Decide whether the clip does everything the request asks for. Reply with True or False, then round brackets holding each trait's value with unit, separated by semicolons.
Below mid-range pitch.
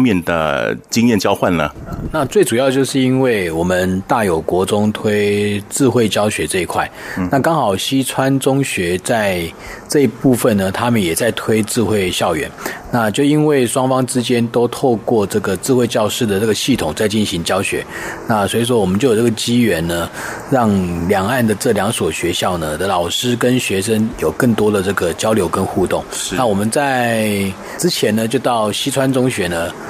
True (115 Hz)